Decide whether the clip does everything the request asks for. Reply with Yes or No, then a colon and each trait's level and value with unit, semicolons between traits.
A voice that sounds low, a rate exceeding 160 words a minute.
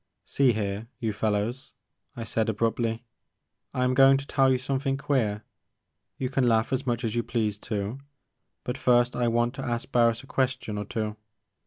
Yes: low, 120 Hz; average, 180 wpm